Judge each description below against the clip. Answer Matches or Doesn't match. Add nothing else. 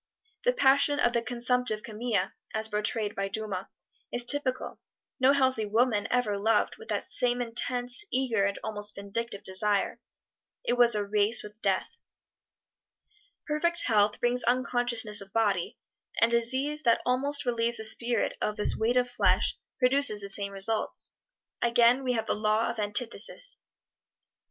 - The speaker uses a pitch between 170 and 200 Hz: Doesn't match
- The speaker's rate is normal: Matches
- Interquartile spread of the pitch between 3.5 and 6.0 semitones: Doesn't match